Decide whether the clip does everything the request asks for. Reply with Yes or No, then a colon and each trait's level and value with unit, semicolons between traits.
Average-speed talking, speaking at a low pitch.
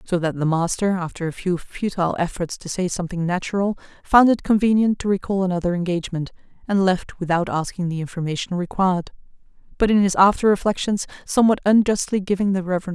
No: average, 170 wpm; medium, 185 Hz